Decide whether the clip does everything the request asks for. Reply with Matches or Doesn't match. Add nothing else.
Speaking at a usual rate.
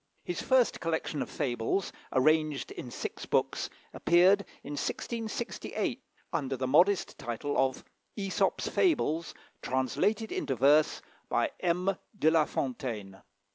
Doesn't match